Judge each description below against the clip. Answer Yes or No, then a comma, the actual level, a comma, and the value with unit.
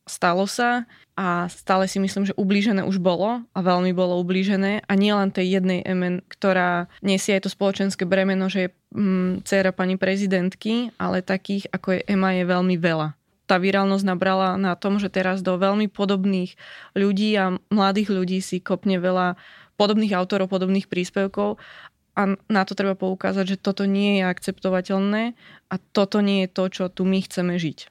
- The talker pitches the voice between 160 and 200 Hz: Yes, high, 190 Hz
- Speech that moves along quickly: Yes, fast, 170 wpm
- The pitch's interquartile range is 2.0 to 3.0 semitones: No, narrow, 1.3 semitones